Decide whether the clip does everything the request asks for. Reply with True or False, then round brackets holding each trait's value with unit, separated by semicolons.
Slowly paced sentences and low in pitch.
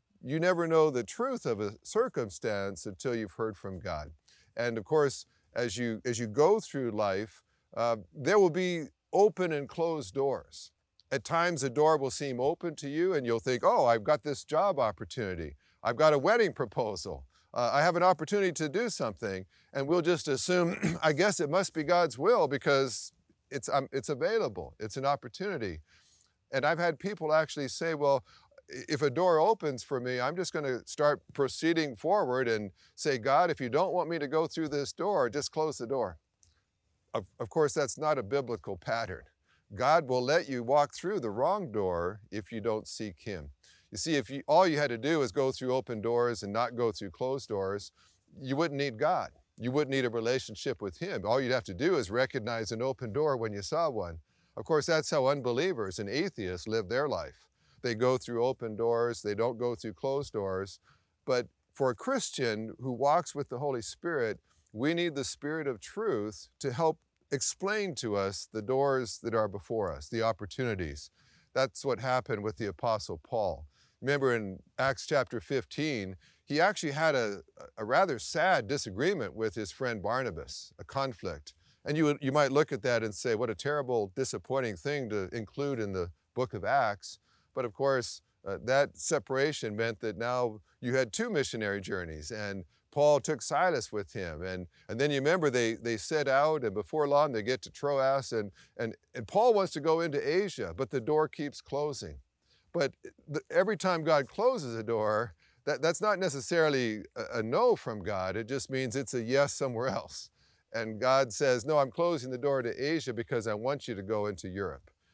False (195 wpm; 125 Hz)